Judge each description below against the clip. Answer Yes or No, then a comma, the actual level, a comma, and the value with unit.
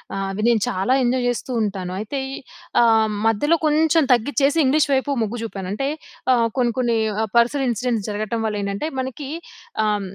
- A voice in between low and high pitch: No, high, 235 Hz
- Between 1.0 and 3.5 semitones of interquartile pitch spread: No, average, 4.2 semitones